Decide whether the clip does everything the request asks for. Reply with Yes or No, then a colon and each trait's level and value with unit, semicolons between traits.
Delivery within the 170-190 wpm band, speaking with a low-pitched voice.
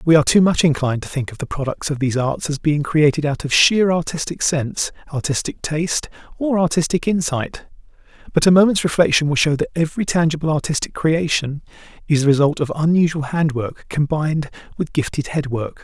No: average, 185 wpm; medium, 155 Hz